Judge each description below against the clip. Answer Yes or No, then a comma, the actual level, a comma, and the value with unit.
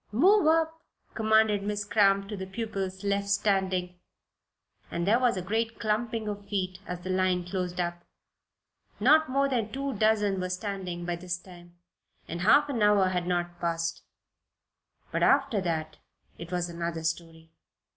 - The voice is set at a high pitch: Yes, high, 195 Hz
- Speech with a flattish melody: No, average, 3.6 semitones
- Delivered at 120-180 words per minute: Yes, average, 155 wpm